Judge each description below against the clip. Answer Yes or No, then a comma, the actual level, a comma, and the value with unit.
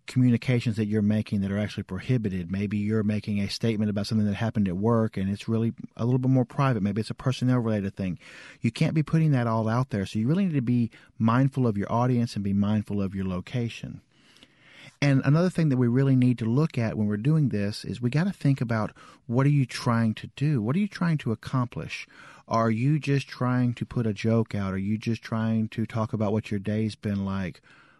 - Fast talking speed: Yes, fast, 235 wpm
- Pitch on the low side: Yes, low, 115 Hz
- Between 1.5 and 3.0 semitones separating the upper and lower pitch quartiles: No, average, 3.4 semitones